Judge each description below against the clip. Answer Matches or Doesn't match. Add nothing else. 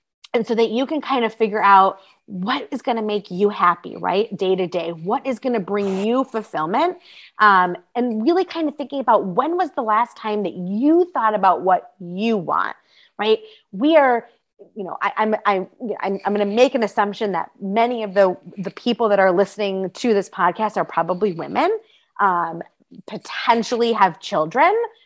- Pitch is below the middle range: Doesn't match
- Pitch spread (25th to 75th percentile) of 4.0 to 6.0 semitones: Matches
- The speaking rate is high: Doesn't match